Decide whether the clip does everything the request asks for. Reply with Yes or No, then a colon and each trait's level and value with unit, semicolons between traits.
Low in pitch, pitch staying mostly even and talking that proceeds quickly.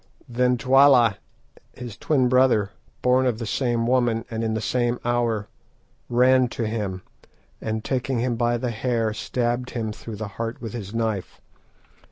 No: low, 120 Hz; narrow, 2.1 semitones; average, 165 wpm